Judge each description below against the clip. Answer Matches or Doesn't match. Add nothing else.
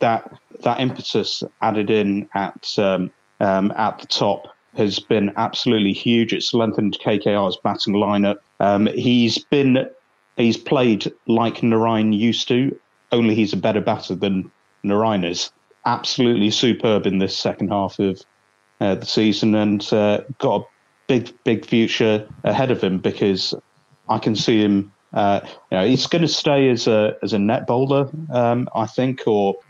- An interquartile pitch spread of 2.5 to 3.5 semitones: Matches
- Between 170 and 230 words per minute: Doesn't match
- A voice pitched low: Matches